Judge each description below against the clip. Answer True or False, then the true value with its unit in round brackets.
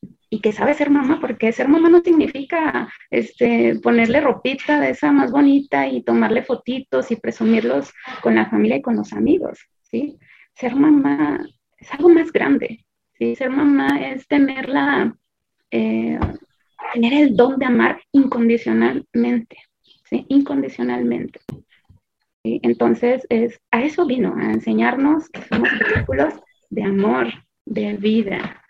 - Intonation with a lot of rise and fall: True (6.3 semitones)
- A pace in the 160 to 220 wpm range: False (135 wpm)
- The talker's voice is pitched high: True (250 Hz)